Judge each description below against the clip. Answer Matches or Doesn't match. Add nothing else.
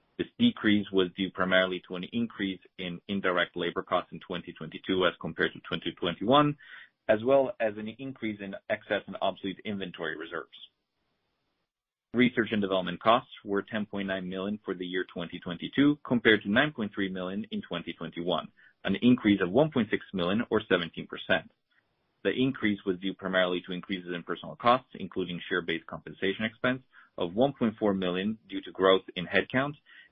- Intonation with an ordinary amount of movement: Matches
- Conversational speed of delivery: Matches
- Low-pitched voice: Matches